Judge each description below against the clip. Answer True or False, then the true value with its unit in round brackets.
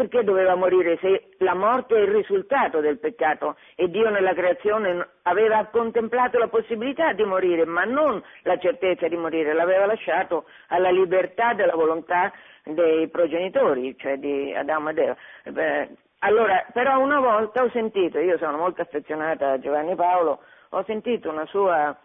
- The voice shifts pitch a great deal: True (6.0 semitones)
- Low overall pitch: False (185 Hz)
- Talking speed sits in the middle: True (155 wpm)